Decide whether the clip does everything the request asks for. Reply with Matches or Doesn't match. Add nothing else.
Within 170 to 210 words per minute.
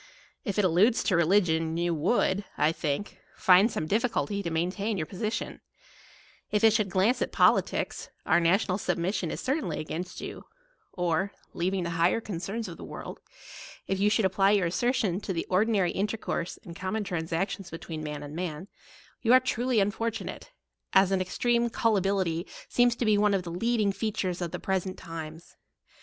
Matches